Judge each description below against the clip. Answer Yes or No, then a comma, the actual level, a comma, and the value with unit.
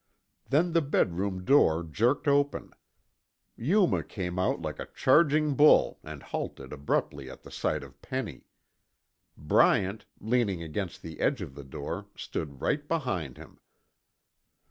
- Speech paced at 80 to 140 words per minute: Yes, slow, 135 wpm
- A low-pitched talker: Yes, low, 100 Hz